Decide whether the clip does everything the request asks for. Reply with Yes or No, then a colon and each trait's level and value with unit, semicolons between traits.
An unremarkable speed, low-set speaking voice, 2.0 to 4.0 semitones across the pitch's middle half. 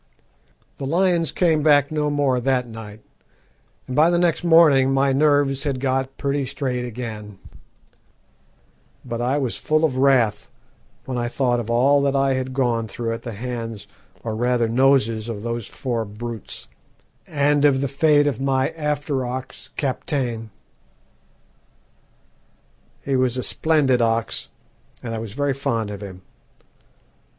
Yes: average, 145 wpm; low, 130 Hz; average, 3.4 semitones